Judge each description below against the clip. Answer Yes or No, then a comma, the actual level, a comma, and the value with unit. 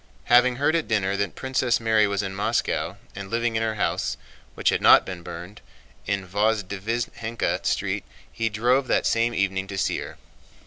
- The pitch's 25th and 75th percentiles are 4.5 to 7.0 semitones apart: No, average, 3.2 semitones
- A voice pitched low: Yes, low, 110 Hz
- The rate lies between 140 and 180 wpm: Yes, average, 165 wpm